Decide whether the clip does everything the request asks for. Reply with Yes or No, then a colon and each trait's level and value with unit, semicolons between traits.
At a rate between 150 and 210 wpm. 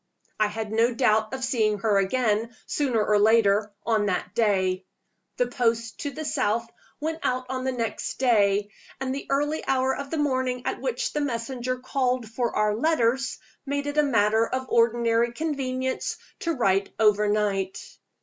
Yes: average, 165 wpm